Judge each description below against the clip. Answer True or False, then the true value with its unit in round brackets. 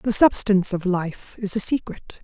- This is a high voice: True (200 Hz)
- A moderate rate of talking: True (190 wpm)